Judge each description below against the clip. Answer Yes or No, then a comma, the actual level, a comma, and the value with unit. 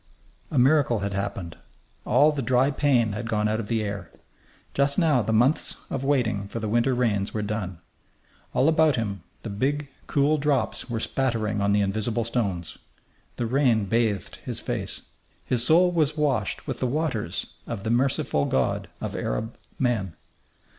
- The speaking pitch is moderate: No, low, 115 Hz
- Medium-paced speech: Yes, average, 165 wpm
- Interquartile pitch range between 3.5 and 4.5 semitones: No, average, 4.9 semitones